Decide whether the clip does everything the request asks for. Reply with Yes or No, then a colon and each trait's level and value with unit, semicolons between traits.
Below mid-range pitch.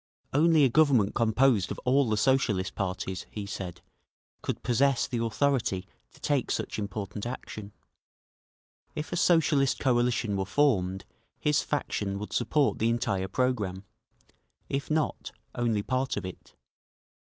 Yes: low, 120 Hz